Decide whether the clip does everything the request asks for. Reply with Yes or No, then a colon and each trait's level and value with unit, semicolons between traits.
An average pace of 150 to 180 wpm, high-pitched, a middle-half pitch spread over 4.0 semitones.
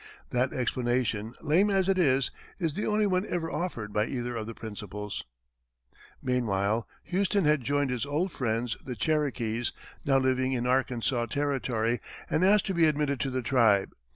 No: average, 165 wpm; low, 130 Hz; average, 4.7 semitones